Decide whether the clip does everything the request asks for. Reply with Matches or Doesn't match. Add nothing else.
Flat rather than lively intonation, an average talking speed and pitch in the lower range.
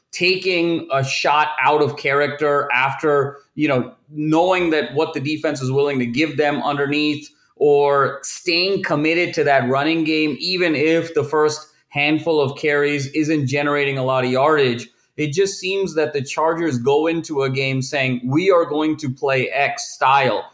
Doesn't match